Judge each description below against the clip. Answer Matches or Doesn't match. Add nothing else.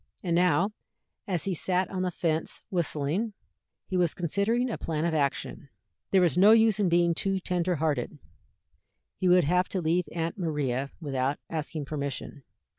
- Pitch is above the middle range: Doesn't match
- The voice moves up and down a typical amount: Matches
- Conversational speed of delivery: Matches